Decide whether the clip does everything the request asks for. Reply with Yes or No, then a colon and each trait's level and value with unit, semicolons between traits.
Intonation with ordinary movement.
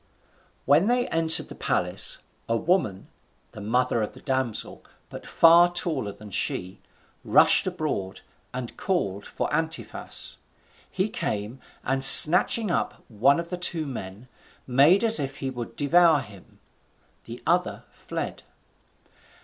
No: wide, 7.2 semitones